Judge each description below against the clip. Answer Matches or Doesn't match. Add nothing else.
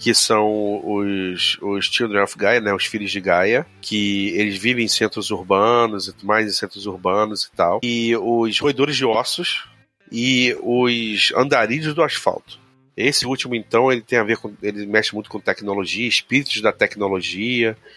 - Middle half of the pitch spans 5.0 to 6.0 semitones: Doesn't match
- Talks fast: Doesn't match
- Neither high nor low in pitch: Doesn't match